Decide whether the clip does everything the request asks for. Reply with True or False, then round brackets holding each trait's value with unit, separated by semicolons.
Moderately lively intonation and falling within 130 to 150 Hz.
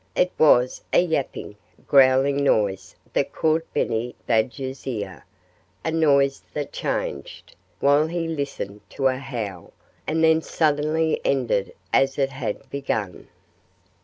True (4.4 semitones; 135 Hz)